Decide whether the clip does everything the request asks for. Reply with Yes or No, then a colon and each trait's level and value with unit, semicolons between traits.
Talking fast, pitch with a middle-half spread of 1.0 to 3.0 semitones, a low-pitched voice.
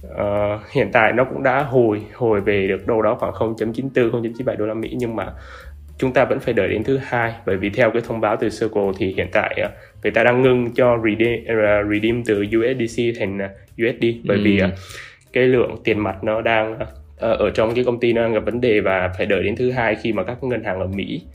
No: average, 240 wpm; narrow, 2.5 semitones; low, 110 Hz